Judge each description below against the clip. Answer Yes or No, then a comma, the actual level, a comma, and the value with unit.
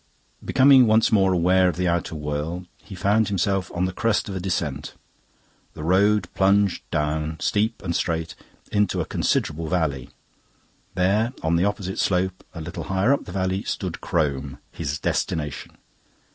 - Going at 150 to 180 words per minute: Yes, average, 160 wpm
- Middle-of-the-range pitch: No, very low, 90 Hz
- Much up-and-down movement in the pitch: No, average, 3.5 semitones